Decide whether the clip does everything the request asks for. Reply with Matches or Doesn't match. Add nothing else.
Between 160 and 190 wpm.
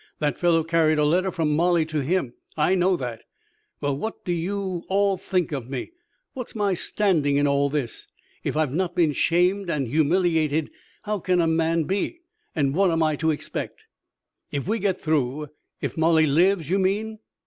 Matches